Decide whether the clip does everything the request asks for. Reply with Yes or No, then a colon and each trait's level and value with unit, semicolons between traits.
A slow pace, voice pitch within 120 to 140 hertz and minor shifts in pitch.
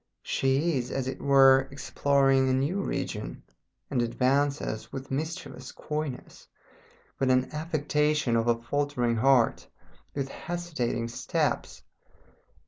Yes: slow, 115 wpm; low, 135 Hz; narrow, 2.3 semitones